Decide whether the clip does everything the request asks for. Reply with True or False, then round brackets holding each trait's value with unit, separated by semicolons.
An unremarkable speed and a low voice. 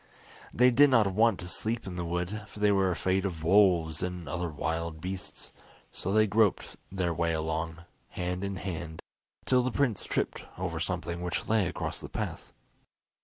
True (175 wpm; 90 Hz)